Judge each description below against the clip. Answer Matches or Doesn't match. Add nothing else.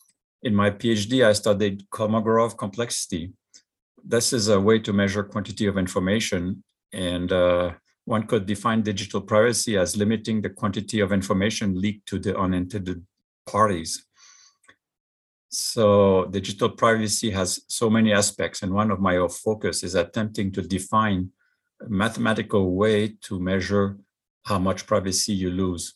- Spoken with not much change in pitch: Matches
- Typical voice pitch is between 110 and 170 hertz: Doesn't match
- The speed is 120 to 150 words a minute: Matches